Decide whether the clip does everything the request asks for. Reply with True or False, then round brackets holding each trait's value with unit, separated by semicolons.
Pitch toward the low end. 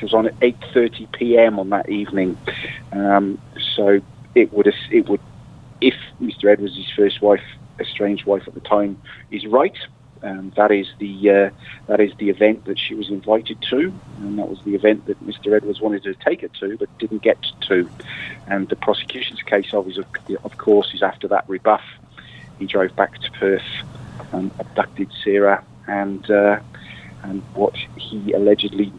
True (105 Hz)